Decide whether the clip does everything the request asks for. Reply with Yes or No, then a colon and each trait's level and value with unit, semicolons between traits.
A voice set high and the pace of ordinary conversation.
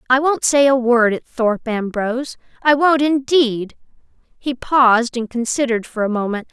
Yes: high, 245 Hz; average, 165 wpm